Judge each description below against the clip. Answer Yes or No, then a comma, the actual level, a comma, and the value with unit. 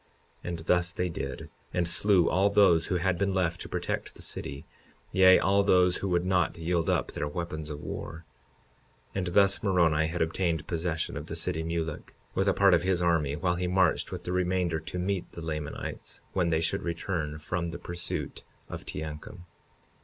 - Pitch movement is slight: Yes, narrow, 2.1 semitones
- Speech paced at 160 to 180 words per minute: No, average, 195 wpm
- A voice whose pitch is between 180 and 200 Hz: No, very low, 85 Hz